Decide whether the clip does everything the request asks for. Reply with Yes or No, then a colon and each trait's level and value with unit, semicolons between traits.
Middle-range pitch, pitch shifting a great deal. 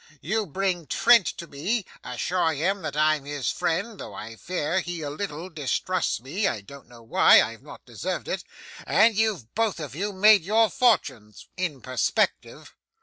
Yes: medium, 170 Hz; wide, 6.2 semitones